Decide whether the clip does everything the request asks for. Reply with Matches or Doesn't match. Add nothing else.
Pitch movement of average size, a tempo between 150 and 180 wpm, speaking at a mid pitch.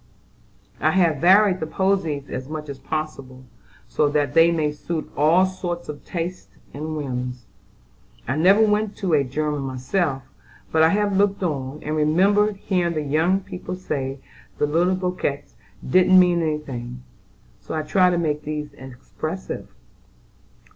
Matches